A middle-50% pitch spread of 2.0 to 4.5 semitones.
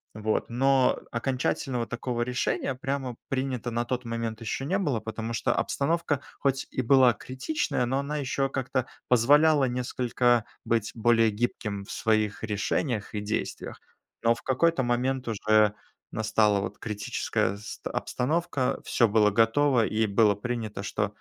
Yes: average, 3.2 semitones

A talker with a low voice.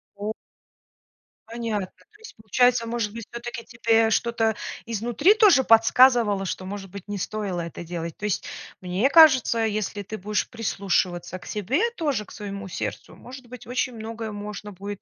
No: high, 215 Hz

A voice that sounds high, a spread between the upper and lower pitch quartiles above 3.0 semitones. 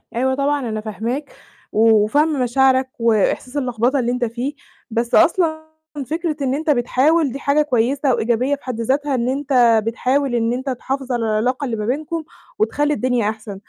Yes: very high, 255 Hz; average, 3.4 semitones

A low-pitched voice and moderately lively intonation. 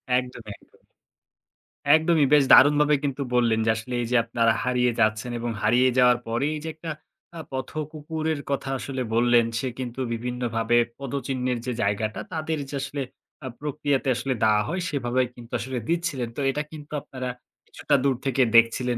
Yes: low, 125 Hz; average, 3.4 semitones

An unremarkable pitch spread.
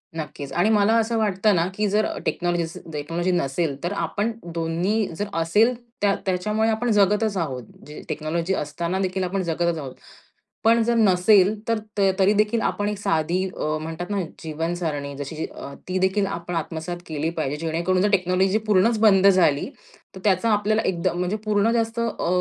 Yes: average, 4.0 semitones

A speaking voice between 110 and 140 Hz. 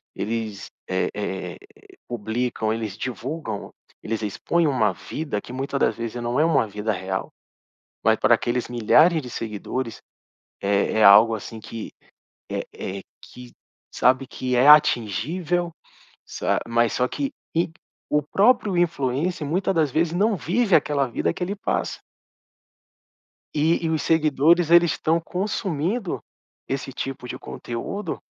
Yes: low, 135 Hz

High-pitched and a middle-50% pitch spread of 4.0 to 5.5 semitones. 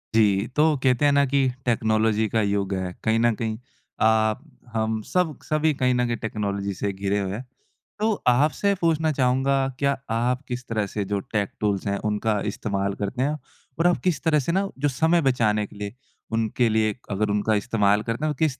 No: low, 115 Hz; average, 5.0 semitones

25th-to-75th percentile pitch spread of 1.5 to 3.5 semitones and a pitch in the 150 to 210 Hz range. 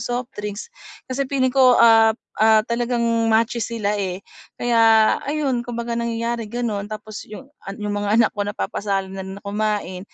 No: narrow, 2.5 semitones; high, 225 Hz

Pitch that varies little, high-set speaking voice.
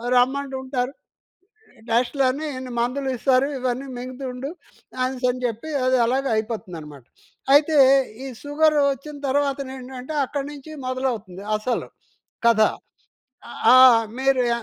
Yes: narrow, 1.9 semitones; very high, 260 Hz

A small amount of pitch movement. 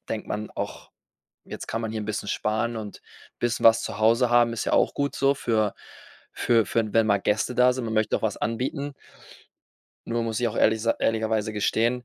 Yes: narrow, 1.7 semitones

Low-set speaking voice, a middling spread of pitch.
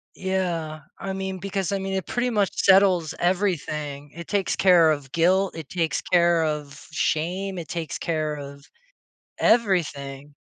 No: medium, 170 Hz; average, 3.8 semitones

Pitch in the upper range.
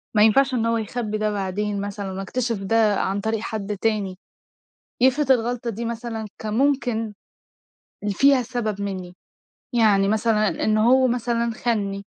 Yes: high, 220 Hz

